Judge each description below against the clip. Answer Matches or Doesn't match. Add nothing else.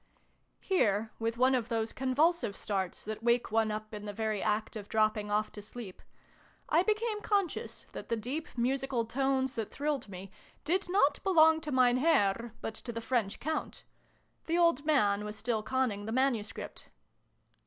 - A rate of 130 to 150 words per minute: Doesn't match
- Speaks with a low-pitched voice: Doesn't match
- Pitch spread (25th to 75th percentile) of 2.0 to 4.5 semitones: Doesn't match